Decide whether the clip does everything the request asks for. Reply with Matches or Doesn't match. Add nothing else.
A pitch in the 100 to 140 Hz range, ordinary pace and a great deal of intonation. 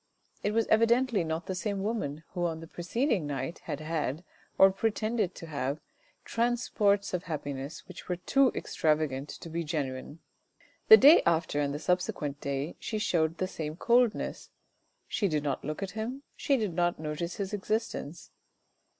Doesn't match